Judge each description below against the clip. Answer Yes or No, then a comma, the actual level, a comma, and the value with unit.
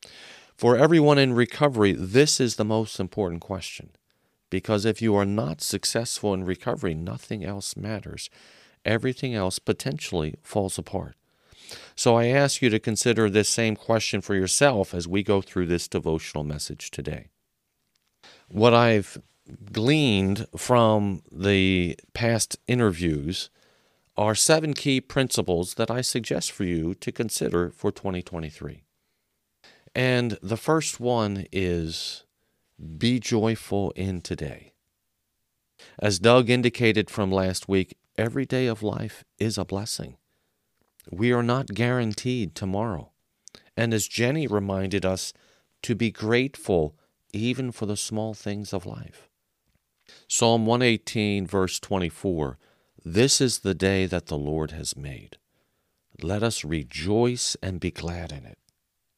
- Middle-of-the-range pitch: No, low, 105 Hz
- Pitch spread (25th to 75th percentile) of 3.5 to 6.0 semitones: Yes, average, 4.2 semitones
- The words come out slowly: Yes, slow, 130 wpm